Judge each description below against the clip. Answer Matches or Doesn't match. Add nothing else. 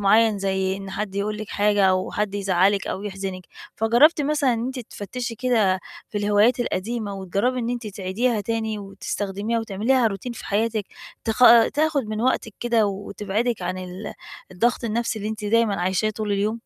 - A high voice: Matches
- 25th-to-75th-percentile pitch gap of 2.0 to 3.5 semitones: Matches